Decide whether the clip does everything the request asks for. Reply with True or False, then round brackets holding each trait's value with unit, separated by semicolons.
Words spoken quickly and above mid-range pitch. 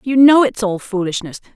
False (190 wpm; 220 Hz)